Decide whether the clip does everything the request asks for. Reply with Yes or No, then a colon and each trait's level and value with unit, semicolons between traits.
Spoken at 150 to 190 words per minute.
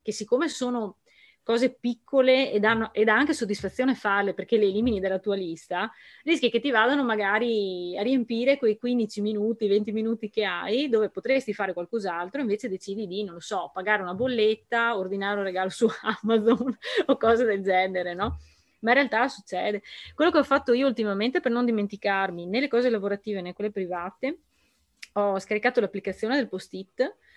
Yes: fast, 170 wpm